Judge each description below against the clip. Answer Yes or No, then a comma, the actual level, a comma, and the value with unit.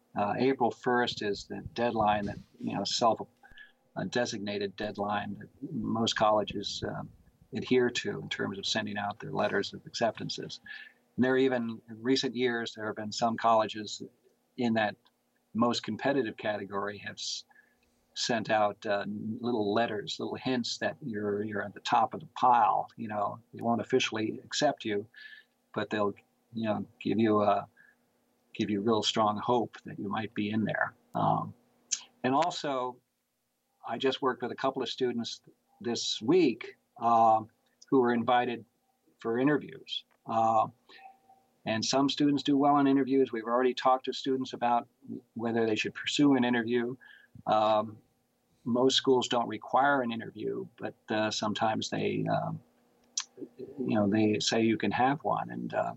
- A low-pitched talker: Yes, low, 115 Hz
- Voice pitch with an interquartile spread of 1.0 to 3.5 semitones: Yes, average, 3.0 semitones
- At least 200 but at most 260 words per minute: No, average, 160 wpm